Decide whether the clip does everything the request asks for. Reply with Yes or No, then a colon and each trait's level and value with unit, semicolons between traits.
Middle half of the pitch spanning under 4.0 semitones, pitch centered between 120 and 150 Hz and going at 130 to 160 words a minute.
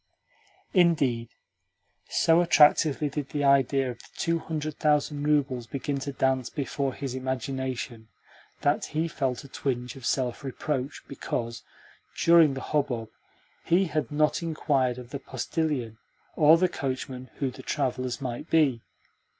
Yes: average, 3.0 semitones; medium, 140 Hz; average, 140 wpm